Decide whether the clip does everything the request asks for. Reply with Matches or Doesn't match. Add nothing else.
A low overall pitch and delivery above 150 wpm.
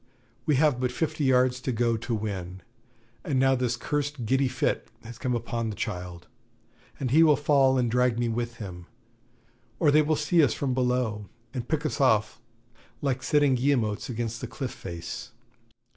Matches